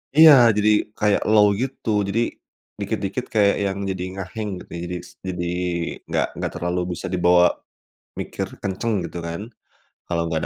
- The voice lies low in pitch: Yes, low, 100 Hz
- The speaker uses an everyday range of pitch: Yes, average, 3.4 semitones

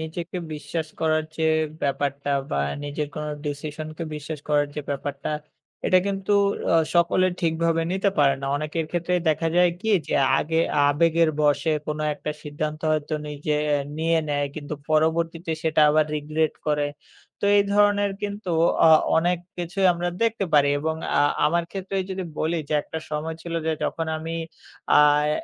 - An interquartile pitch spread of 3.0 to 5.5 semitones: No, narrow, 2.4 semitones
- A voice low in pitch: No, medium, 160 Hz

